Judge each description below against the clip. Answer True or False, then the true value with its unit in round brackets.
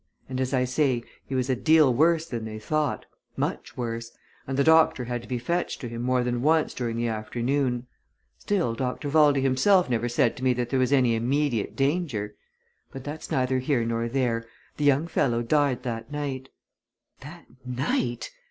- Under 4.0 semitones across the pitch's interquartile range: True (3.3 semitones)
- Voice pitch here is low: True (130 Hz)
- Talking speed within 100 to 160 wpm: False (185 wpm)